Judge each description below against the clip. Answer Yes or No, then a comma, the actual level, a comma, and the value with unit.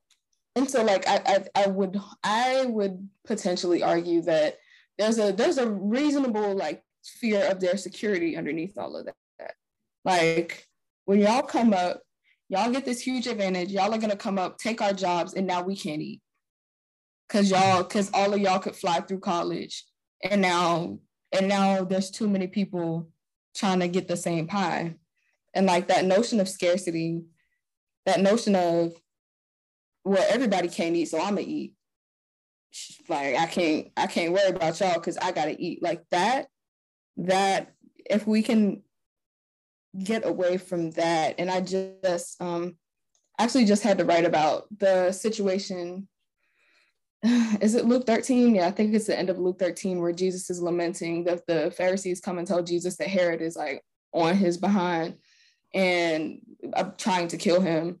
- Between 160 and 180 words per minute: Yes, average, 165 wpm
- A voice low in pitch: No, high, 190 Hz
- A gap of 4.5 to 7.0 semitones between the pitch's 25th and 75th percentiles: No, average, 2.9 semitones